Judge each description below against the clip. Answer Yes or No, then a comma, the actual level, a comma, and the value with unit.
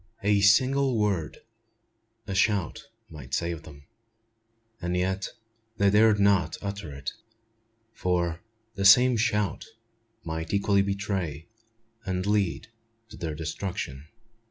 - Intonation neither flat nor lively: Yes, average, 3.8 semitones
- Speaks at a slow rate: Yes, slow, 110 wpm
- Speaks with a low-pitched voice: Yes, low, 100 Hz